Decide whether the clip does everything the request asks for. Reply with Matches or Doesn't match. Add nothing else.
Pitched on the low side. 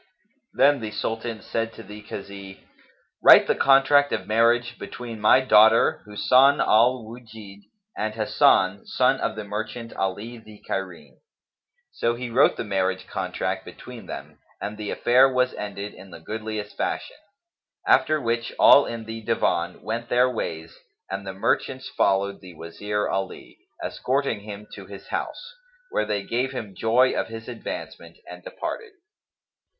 Matches